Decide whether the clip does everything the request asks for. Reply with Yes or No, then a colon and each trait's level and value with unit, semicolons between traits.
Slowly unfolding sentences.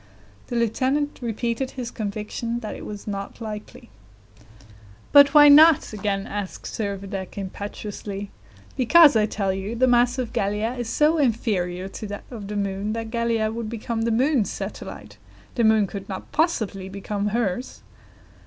No: average, 155 wpm